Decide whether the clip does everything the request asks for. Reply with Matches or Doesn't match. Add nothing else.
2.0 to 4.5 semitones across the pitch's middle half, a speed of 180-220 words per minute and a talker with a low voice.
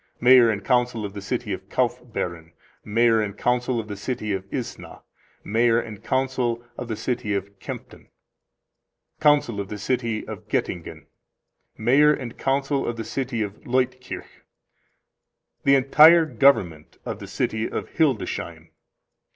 Doesn't match